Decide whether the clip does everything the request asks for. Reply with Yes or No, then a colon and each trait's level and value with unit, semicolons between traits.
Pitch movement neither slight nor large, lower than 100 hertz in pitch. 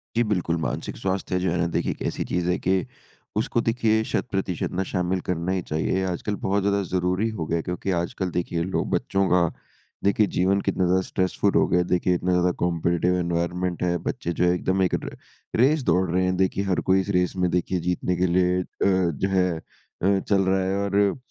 No: narrow, 1.5 semitones; very low, 90 Hz